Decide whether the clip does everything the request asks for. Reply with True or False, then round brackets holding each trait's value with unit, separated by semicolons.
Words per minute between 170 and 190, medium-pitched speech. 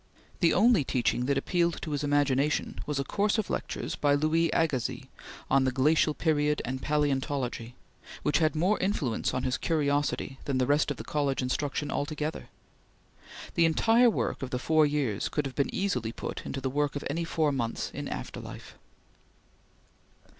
True (175 wpm; 145 Hz)